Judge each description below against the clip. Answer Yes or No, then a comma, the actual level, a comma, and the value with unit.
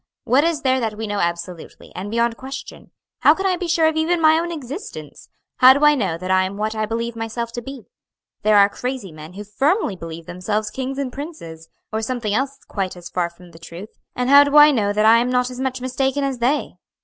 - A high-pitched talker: Yes, high, 235 Hz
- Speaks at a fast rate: Yes, fast, 235 wpm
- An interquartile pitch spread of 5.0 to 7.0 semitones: Yes, wide, 5.4 semitones